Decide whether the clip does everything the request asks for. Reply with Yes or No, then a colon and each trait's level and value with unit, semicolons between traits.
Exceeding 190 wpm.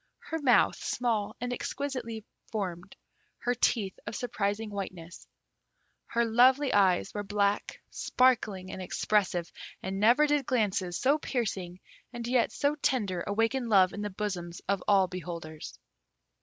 No: slow, 135 wpm